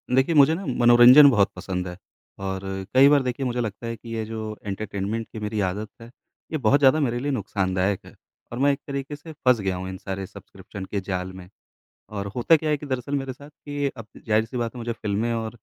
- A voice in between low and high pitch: No, low, 115 Hz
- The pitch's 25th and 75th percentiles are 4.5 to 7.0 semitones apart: Yes, average, 5.2 semitones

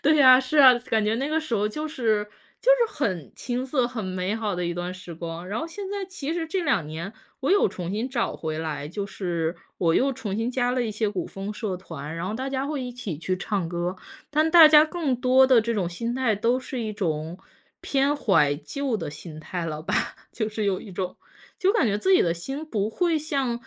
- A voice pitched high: Yes, high, 225 Hz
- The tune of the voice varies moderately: No, wide, 7.0 semitones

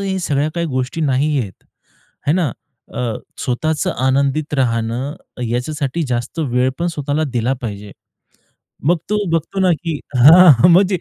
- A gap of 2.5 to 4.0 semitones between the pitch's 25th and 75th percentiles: No, average, 4.9 semitones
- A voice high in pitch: No, medium, 145 Hz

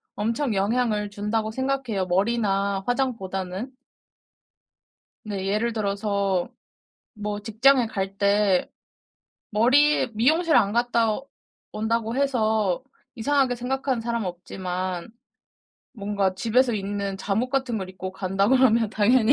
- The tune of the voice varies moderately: Yes, average, 3.7 semitones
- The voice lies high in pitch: Yes, high, 215 Hz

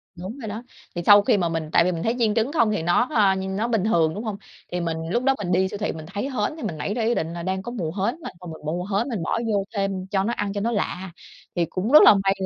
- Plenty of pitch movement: No, average, 3.9 semitones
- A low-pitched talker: No, high, 195 Hz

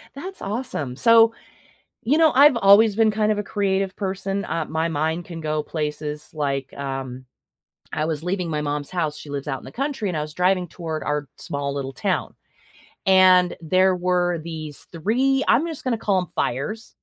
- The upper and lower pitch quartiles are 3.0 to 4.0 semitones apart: No, wide, 5.6 semitones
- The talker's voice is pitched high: No, medium, 180 Hz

